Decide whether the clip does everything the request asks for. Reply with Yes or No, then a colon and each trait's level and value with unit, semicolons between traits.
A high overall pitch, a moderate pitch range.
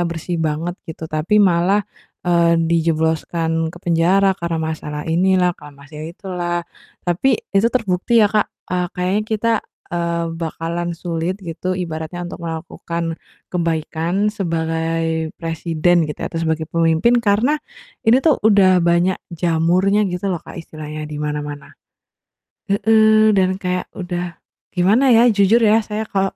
No: medium, 175 Hz; average, 3.2 semitones